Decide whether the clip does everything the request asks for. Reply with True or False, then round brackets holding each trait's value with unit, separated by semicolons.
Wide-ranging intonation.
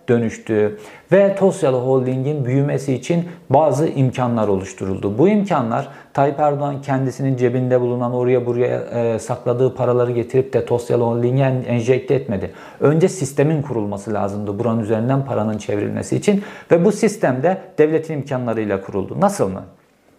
False (4.0 semitones)